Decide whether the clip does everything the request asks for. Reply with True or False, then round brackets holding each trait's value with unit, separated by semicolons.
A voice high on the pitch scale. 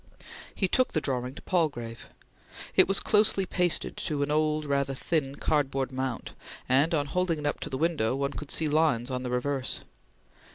False (145 Hz)